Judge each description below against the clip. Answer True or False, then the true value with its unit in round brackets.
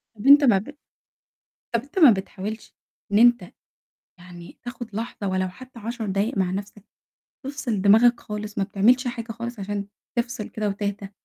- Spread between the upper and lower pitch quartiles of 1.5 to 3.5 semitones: True (3.2 semitones)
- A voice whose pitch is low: False (215 Hz)